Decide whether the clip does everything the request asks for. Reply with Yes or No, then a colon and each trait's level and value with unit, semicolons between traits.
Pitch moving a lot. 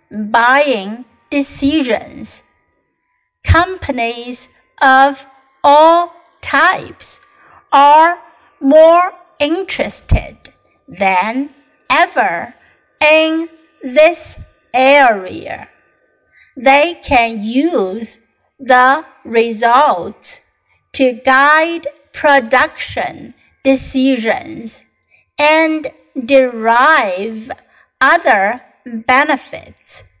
No: average, 3.8 semitones